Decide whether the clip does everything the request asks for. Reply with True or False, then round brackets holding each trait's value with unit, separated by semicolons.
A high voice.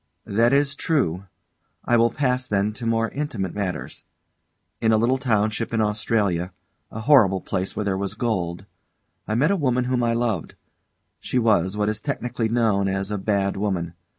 False (110 Hz)